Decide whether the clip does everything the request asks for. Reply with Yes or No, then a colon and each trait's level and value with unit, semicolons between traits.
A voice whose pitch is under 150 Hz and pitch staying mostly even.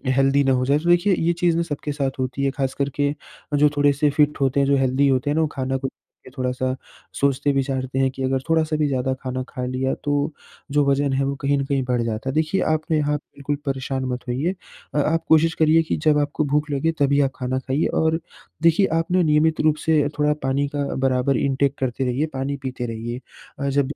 Yes: medium, 140 Hz; narrow, 2.2 semitones